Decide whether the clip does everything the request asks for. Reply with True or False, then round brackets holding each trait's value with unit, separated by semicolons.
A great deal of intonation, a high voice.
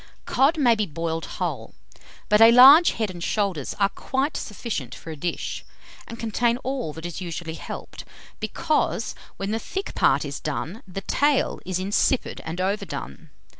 True (6.2 semitones; 205 Hz)